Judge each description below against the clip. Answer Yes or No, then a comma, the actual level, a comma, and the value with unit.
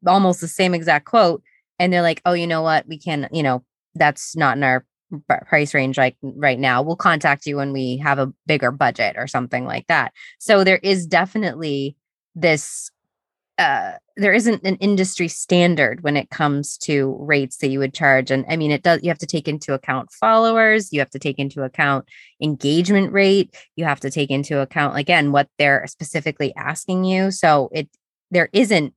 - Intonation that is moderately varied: Yes, average, 4.3 semitones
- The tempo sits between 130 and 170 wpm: No, average, 195 wpm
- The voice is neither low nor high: Yes, medium, 150 Hz